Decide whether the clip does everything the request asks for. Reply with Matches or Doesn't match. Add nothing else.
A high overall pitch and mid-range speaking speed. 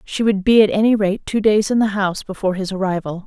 Doesn't match